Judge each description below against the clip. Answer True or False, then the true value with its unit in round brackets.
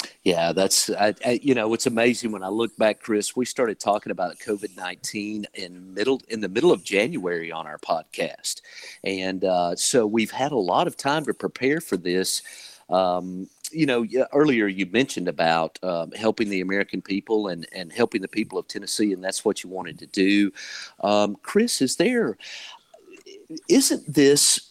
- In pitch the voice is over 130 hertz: False (105 Hz)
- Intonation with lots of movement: True (5.7 semitones)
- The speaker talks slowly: False (175 wpm)